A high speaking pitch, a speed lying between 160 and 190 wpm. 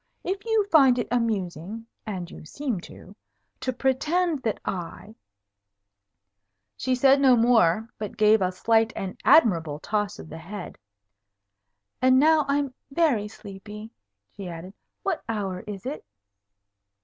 No: high, 220 Hz; average, 140 wpm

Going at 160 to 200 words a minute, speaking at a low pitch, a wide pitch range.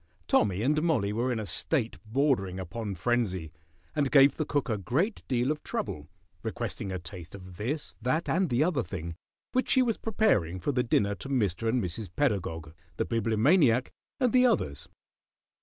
Yes: average, 175 wpm; low, 115 Hz; wide, 7.5 semitones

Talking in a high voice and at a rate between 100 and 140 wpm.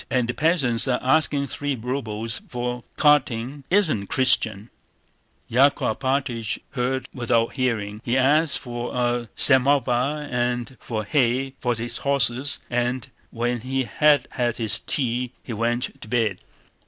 No: low, 125 Hz; slow, 135 wpm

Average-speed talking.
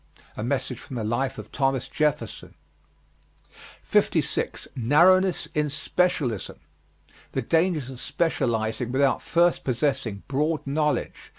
No: slow, 110 wpm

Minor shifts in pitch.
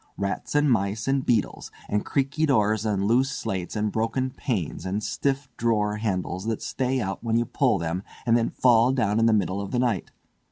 No: average, 4.0 semitones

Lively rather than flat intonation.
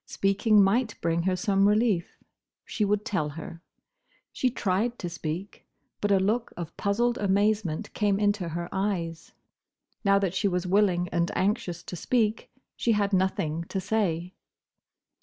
No: average, 3.1 semitones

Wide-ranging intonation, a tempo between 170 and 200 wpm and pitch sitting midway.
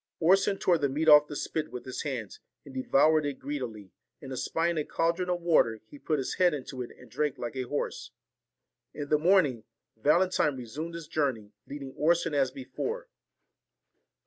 No: average, 4.2 semitones; average, 175 wpm; medium, 145 Hz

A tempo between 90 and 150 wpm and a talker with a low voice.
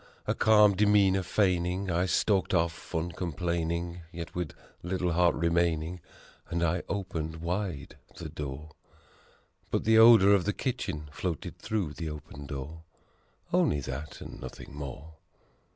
Yes: average, 140 wpm; very low, 85 Hz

